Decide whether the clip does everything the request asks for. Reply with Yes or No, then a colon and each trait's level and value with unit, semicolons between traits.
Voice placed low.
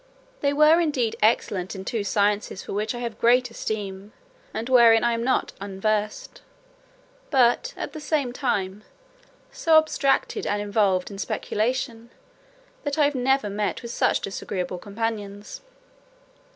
No: high, 225 Hz